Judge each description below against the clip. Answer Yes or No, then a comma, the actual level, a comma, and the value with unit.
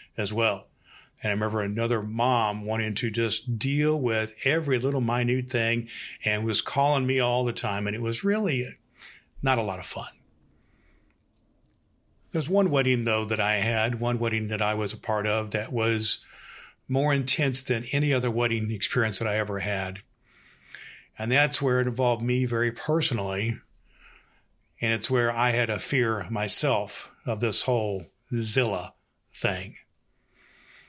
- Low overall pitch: Yes, low, 115 Hz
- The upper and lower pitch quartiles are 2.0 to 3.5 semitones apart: Yes, average, 2.9 semitones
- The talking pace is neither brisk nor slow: Yes, average, 155 wpm